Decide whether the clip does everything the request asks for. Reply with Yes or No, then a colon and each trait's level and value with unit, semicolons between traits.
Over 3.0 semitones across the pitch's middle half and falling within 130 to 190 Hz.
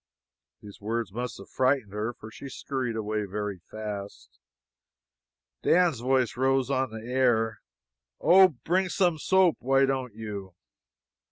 No: average, 4.1 semitones; low, 120 Hz